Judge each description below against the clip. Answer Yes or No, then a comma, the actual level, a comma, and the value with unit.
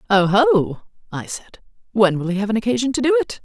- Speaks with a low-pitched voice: No, high, 220 Hz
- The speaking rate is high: No, average, 190 wpm